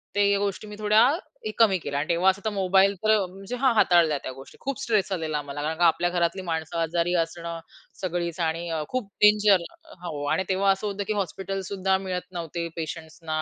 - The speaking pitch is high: No, medium, 180 Hz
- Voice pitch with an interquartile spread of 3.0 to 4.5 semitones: Yes, average, 3.3 semitones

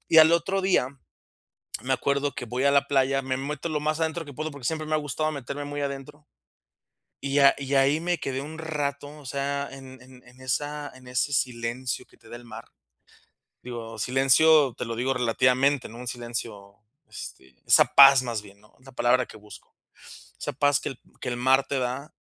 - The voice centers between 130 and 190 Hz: Yes, low, 135 Hz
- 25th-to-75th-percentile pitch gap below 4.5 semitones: Yes, narrow, 2.6 semitones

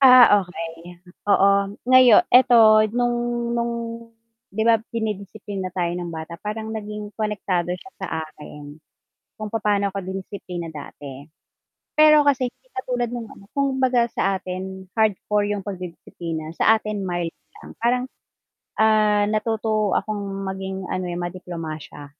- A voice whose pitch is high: Yes, high, 205 Hz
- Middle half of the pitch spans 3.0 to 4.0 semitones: Yes, average, 3.7 semitones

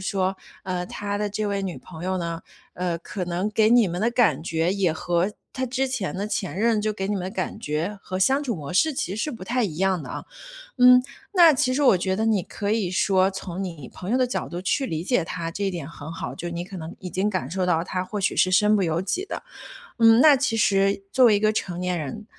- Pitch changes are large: No, average, 3.7 semitones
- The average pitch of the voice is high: Yes, high, 195 Hz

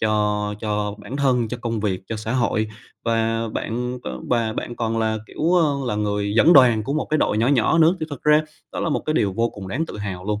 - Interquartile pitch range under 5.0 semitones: Yes, average, 3.8 semitones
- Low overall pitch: Yes, low, 115 Hz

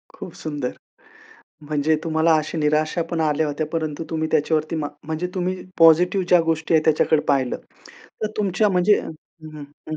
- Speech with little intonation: Yes, narrow, 1.9 semitones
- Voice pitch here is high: No, medium, 160 Hz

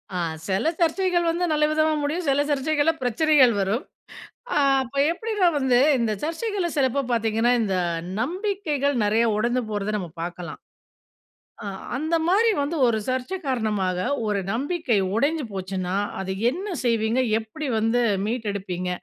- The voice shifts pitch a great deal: Yes, wide, 6.6 semitones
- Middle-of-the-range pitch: No, very high, 260 Hz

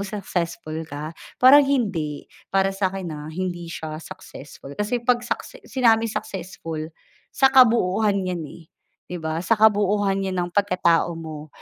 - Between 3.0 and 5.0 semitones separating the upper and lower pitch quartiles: Yes, average, 4.5 semitones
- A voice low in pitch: No, high, 190 Hz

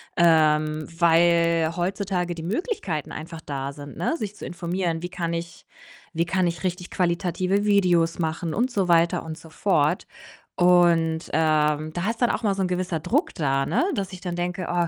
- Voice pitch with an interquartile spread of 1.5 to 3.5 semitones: Yes, narrow, 2.4 semitones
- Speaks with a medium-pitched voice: Yes, medium, 170 Hz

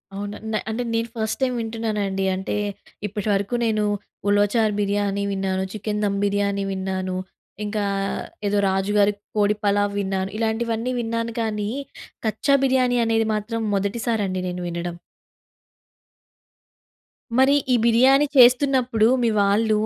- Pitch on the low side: No, high, 210 Hz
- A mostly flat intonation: Yes, narrow, 2.3 semitones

